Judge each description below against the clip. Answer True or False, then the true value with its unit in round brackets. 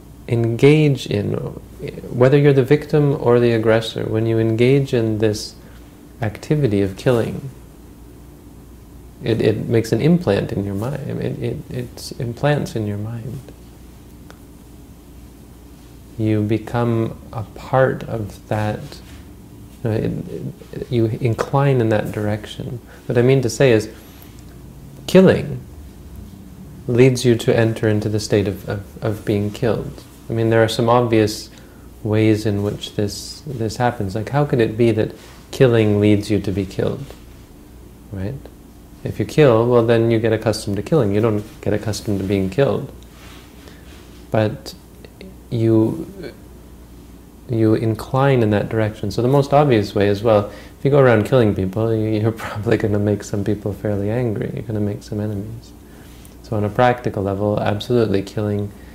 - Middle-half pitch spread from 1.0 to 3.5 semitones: True (2.9 semitones)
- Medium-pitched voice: False (110 Hz)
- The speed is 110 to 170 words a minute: True (155 wpm)